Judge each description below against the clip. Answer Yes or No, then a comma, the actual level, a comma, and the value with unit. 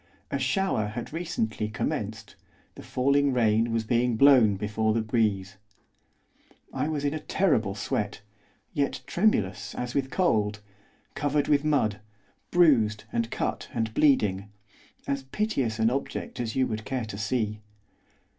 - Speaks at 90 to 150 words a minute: Yes, average, 140 wpm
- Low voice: Yes, low, 115 Hz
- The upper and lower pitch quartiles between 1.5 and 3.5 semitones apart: No, average, 4.7 semitones